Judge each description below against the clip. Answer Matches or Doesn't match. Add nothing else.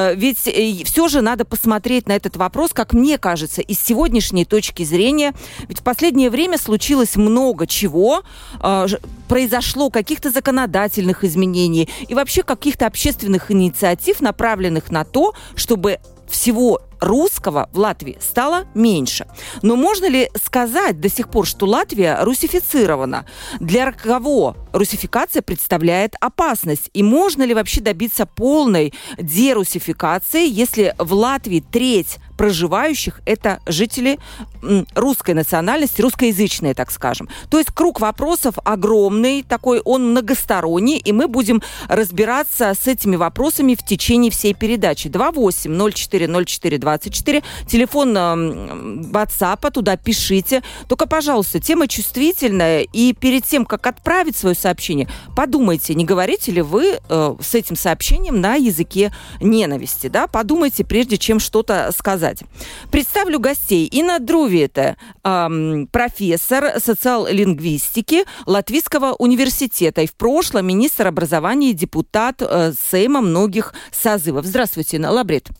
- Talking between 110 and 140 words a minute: Matches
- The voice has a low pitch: Doesn't match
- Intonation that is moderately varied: Doesn't match